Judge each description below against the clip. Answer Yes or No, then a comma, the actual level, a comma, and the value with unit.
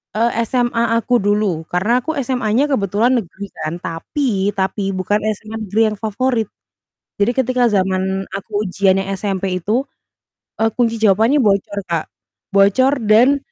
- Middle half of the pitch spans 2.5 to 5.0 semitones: Yes, average, 3.7 semitones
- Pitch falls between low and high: No, high, 210 Hz